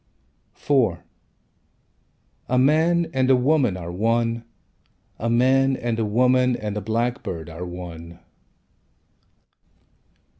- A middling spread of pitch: Yes, average, 4.8 semitones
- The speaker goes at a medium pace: No, slow, 105 wpm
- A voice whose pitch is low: Yes, low, 120 Hz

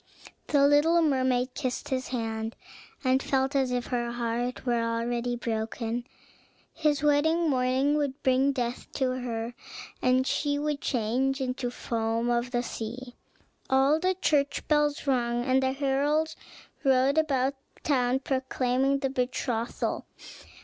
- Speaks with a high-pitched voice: Yes, very high, 260 Hz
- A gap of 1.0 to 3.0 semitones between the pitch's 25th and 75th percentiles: Yes, narrow, 2.5 semitones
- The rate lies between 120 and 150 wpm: Yes, average, 140 wpm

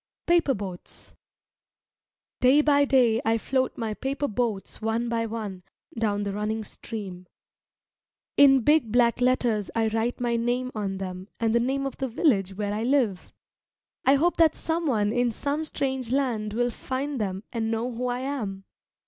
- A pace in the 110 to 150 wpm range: No, average, 165 wpm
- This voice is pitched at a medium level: No, high, 235 Hz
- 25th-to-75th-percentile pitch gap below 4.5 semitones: Yes, average, 3.8 semitones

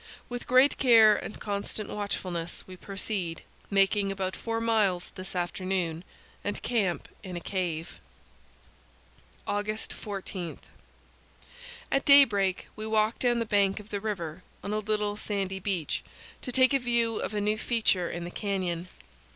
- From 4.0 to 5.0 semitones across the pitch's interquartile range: No, average, 2.9 semitones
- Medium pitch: No, high, 200 Hz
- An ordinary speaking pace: Yes, average, 145 wpm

